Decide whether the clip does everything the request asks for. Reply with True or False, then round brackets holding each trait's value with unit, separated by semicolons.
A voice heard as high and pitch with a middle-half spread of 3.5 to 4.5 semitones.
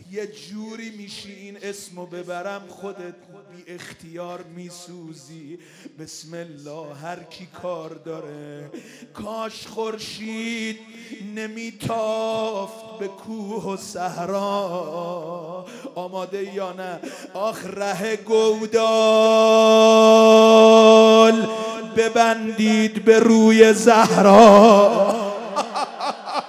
True (205 Hz; 3.8 semitones)